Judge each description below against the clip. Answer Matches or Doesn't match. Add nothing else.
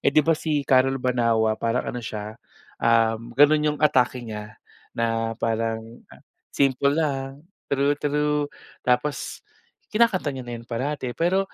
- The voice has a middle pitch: Doesn't match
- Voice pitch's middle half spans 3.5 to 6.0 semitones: Matches